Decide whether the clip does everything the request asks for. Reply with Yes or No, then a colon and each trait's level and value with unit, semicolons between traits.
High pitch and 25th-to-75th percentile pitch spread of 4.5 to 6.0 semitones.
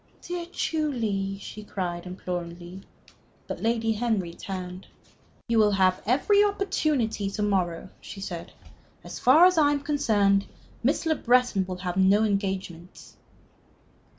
Yes: high, 205 Hz; average, 5.3 semitones